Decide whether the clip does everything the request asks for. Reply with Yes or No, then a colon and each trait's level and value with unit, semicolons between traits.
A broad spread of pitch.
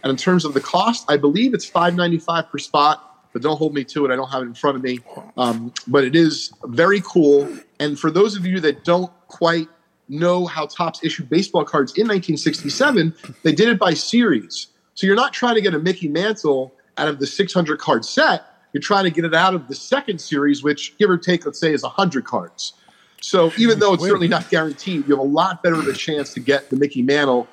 No: average, 4.1 semitones